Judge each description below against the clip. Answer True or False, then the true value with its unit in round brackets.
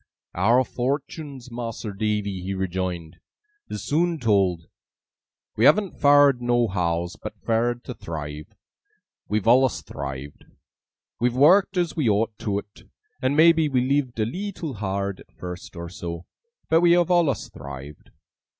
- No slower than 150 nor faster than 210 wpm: False (140 wpm)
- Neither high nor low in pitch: False (115 Hz)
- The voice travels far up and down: True (7.3 semitones)